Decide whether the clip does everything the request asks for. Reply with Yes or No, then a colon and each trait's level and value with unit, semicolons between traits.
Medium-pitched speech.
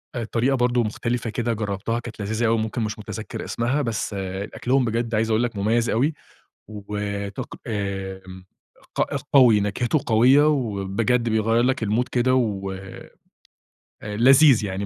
No: low, 115 Hz